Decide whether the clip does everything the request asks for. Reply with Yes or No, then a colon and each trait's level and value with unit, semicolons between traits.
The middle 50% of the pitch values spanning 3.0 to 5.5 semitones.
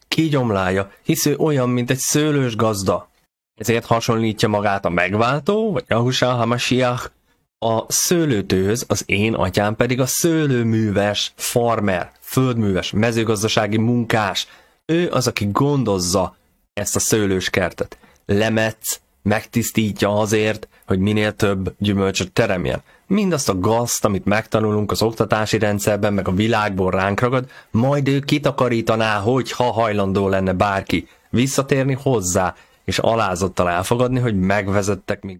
Yes: average, 3.7 semitones